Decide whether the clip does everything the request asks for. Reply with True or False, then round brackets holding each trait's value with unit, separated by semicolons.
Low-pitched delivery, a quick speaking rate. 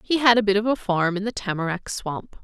False (205 Hz; 270 wpm)